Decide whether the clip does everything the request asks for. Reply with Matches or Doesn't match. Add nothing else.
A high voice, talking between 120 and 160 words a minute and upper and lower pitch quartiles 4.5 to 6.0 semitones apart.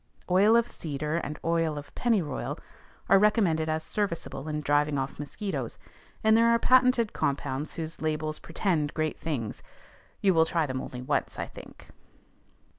Doesn't match